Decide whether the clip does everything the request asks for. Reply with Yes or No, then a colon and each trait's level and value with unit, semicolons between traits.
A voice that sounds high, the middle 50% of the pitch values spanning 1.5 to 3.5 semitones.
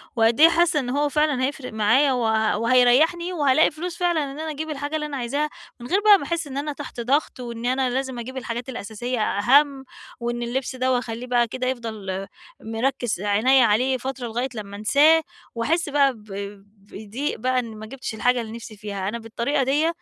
No: very high, 255 Hz; average, 4.0 semitones